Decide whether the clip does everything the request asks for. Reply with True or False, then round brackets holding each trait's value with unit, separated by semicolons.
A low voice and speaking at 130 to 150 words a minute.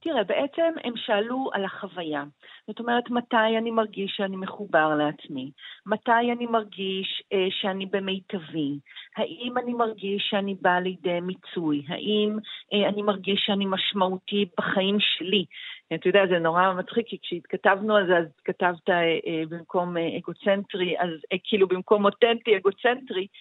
False (195 Hz; 145 wpm)